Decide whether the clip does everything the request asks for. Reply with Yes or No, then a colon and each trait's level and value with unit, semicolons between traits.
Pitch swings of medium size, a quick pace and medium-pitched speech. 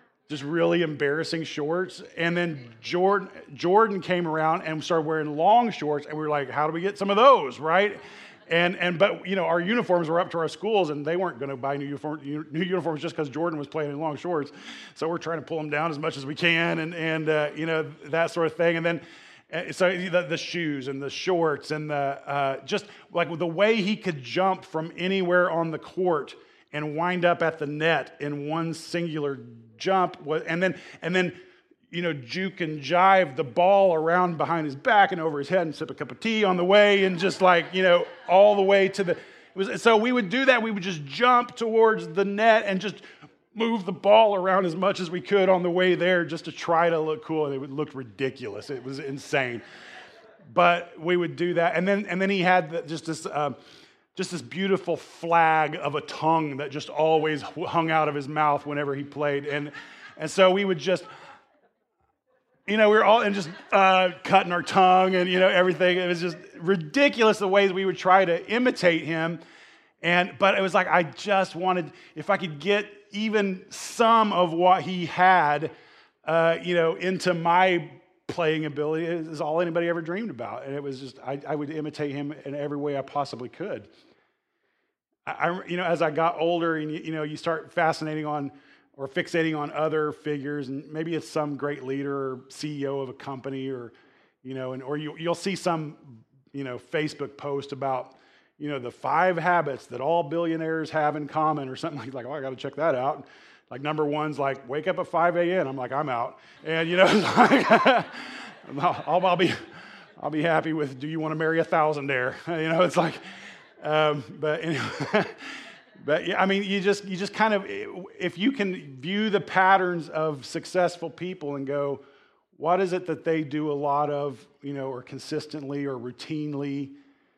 Yes: average, 3.8 semitones; fast, 210 wpm; medium, 165 Hz